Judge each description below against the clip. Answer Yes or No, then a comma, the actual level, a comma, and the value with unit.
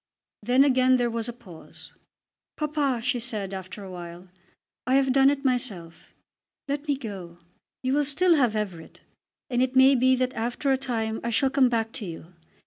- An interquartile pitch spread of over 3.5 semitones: Yes, average, 4.1 semitones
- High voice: Yes, high, 245 Hz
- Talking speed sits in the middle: Yes, average, 185 wpm